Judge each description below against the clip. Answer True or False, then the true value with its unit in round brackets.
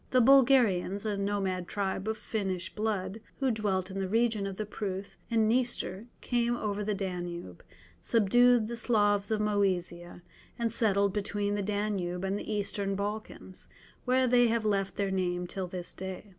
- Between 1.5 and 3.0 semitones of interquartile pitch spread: True (2.5 semitones)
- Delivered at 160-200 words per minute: True (165 wpm)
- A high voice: True (205 Hz)